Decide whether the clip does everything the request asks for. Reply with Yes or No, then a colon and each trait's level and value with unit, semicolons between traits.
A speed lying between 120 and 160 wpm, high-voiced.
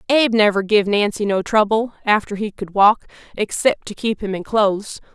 No: average, 185 wpm; high, 210 Hz